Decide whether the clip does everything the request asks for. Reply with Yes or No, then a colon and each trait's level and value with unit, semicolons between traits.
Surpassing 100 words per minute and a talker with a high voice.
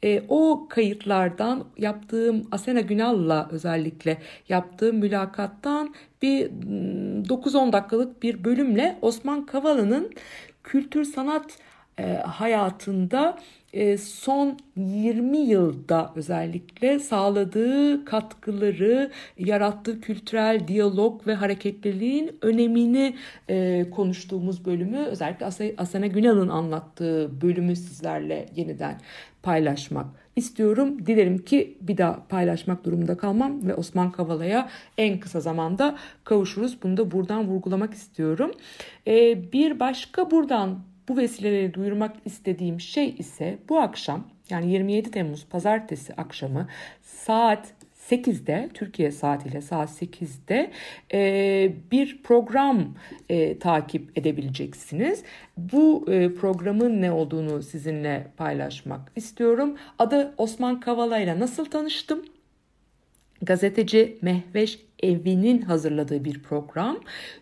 No: slow, 95 wpm; high, 205 Hz